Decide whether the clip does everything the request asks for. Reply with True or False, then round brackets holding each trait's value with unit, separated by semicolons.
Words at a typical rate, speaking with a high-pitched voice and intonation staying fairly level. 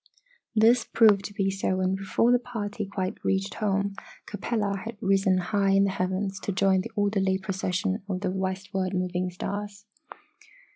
True (155 wpm; 195 Hz; 1.5 semitones)